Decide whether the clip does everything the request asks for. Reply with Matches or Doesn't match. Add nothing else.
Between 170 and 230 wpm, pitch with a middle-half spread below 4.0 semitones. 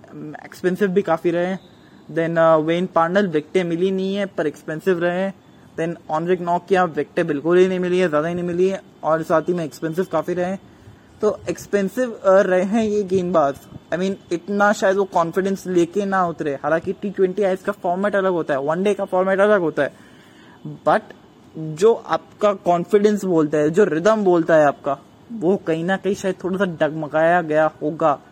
Matches